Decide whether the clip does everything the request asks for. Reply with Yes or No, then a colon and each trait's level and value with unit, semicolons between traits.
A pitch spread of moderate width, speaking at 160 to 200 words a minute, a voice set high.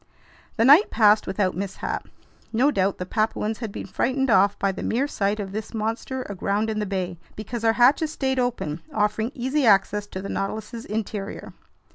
Yes: average, 3.4 semitones; average, 180 wpm; high, 215 Hz